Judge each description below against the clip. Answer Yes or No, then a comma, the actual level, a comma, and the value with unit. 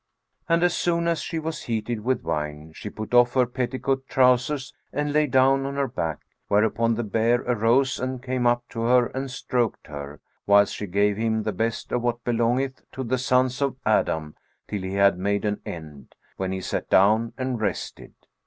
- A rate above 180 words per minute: Yes, average, 190 wpm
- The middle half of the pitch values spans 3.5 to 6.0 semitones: Yes, average, 4.0 semitones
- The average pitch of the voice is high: No, low, 120 Hz